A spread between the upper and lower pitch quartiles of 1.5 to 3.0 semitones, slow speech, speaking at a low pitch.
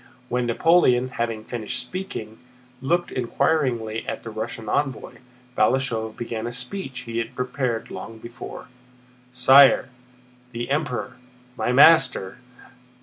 Yes: narrow, 2.6 semitones; slow, 115 wpm; low, 125 Hz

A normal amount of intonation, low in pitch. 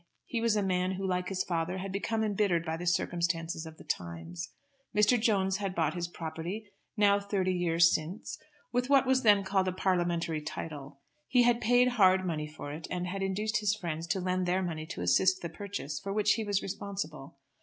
No: average, 3.6 semitones; medium, 185 Hz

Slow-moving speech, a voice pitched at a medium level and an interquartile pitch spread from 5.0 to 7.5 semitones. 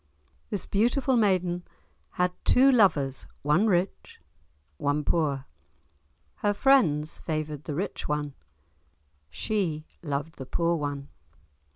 Yes: slow, 105 wpm; medium, 165 Hz; wide, 5.5 semitones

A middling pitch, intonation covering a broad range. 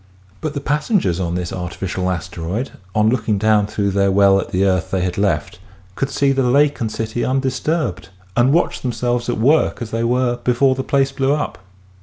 No: low, 115 Hz; wide, 5.9 semitones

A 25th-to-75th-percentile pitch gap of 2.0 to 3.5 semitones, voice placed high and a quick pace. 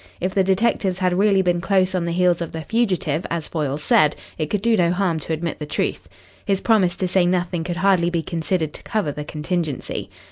No: average, 2.8 semitones; medium, 175 Hz; fast, 220 wpm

